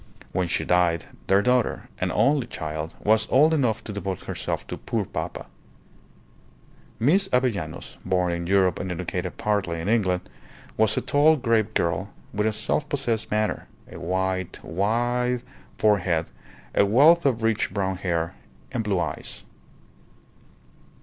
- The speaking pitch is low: Yes, low, 100 Hz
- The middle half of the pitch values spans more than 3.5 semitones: Yes, average, 5.0 semitones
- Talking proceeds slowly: No, average, 145 wpm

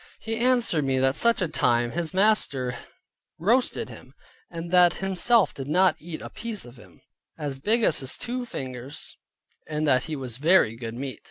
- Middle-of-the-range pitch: Yes, medium, 155 Hz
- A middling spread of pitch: No, wide, 7.9 semitones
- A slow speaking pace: No, average, 175 wpm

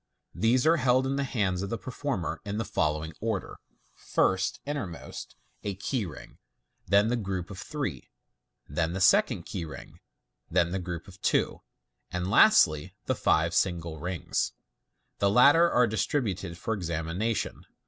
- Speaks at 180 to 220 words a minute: No, average, 160 wpm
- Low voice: Yes, low, 100 Hz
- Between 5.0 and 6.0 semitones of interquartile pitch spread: Yes, wide, 5.6 semitones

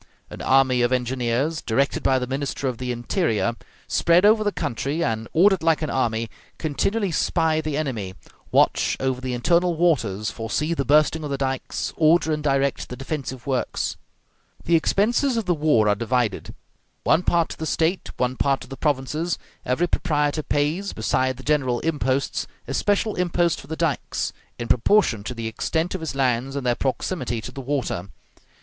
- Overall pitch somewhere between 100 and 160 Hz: Yes, medium, 140 Hz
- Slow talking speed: No, average, 180 wpm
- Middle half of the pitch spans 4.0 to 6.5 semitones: Yes, average, 4.6 semitones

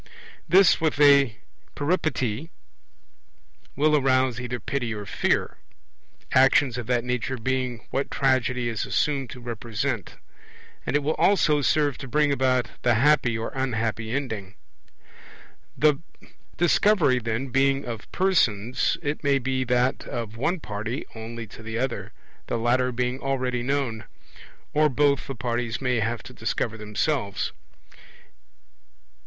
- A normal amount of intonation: Yes, average, 3.3 semitones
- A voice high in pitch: No, low, 125 Hz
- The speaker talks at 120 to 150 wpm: Yes, slow, 135 wpm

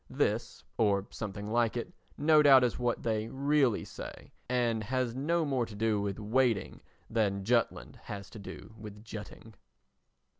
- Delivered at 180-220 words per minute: No, average, 155 wpm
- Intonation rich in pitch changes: No, average, 3.5 semitones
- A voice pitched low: Yes, low, 115 Hz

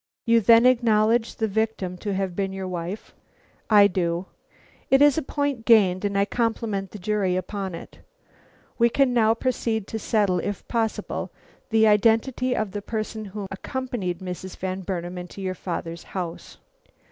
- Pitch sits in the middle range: No, high, 210 Hz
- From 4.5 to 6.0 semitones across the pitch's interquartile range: No, average, 3.4 semitones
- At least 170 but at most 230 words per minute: No, average, 160 wpm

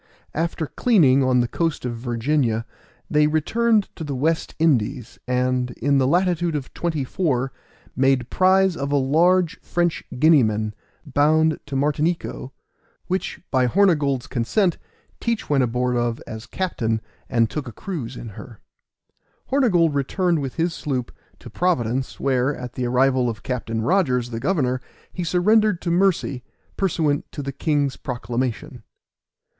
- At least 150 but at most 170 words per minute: No, average, 140 wpm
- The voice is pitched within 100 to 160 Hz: Yes, medium, 140 Hz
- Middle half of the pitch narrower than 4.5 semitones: No, average, 5.2 semitones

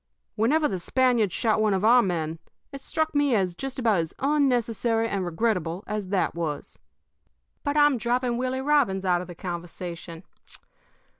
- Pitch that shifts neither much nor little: No, wide, 6.2 semitones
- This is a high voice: Yes, high, 220 Hz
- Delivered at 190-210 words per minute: No, average, 160 wpm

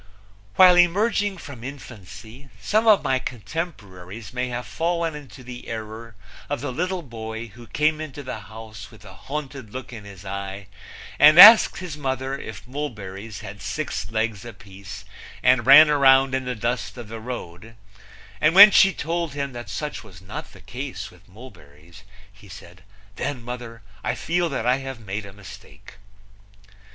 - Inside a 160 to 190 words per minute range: Yes, average, 165 wpm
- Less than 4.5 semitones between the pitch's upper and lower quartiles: No, wide, 5.5 semitones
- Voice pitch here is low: Yes, low, 125 Hz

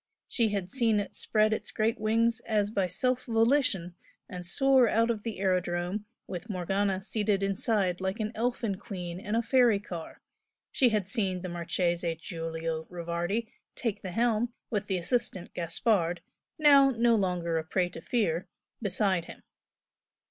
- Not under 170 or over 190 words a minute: No, average, 155 wpm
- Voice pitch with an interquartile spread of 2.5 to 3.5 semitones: No, average, 4.3 semitones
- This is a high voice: Yes, high, 200 Hz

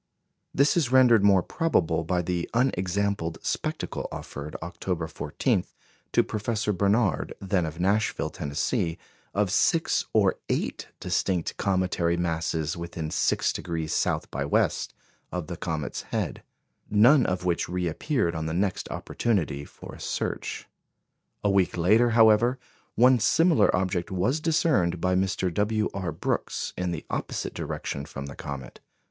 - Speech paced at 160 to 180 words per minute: No, average, 140 wpm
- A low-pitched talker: Yes, very low, 90 Hz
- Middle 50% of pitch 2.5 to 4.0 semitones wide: No, average, 4.4 semitones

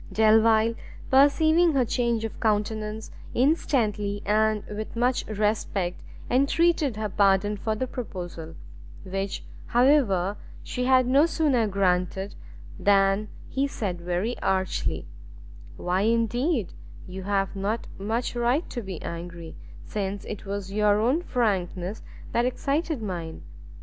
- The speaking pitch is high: Yes, high, 215 Hz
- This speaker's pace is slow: Yes, slow, 120 wpm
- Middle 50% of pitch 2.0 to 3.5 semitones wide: No, average, 4.1 semitones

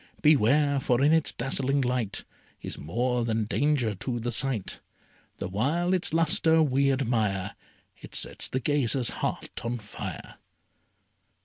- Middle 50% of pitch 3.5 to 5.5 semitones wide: Yes, average, 4.0 semitones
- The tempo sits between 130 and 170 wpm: Yes, slow, 135 wpm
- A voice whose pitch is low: Yes, low, 130 Hz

